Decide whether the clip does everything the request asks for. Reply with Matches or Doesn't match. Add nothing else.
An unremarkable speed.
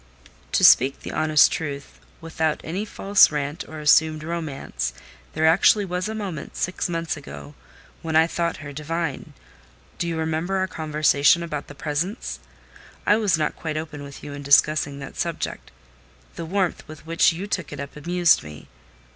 Matches